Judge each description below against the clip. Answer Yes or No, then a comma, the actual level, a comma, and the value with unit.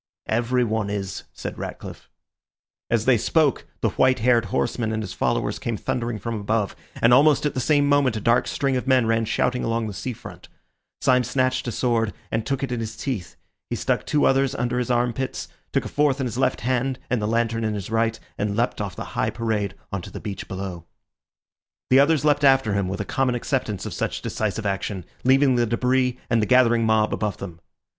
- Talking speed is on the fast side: Yes, fast, 210 wpm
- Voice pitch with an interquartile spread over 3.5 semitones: No, average, 3.2 semitones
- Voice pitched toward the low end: Yes, low, 115 Hz